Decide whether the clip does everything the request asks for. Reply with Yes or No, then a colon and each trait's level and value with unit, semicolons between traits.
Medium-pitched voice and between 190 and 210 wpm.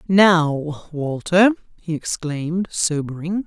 No: medium, 165 Hz; slow, 85 wpm